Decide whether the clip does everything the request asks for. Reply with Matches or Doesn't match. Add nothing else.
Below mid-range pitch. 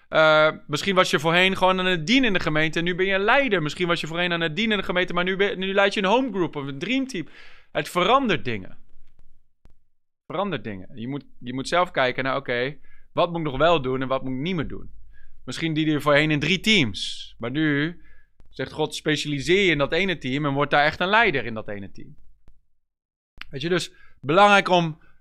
Doesn't match